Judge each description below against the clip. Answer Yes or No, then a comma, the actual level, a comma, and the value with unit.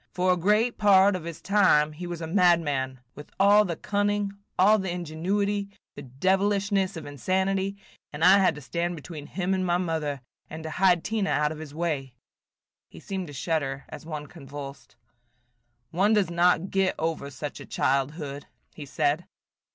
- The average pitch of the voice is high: No, medium, 175 Hz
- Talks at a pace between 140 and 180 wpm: Yes, average, 175 wpm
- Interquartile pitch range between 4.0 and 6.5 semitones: Yes, average, 4.5 semitones